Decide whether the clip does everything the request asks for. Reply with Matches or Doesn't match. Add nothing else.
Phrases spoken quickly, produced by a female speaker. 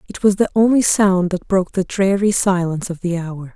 Matches